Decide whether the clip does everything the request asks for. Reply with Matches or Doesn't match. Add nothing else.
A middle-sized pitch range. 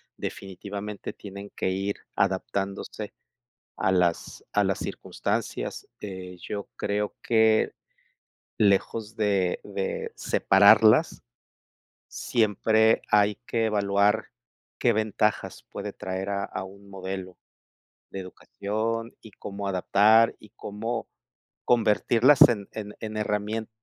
Doesn't match